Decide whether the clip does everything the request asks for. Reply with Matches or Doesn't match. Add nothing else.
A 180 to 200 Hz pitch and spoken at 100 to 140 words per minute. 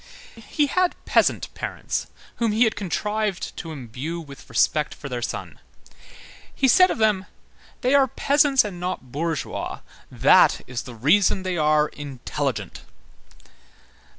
Matches